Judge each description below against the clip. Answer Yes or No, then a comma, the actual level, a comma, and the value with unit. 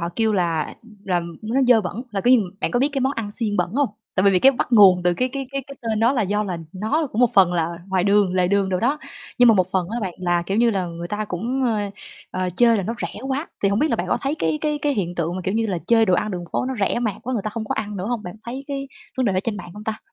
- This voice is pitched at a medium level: No, high, 210 Hz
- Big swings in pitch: No, average, 4.6 semitones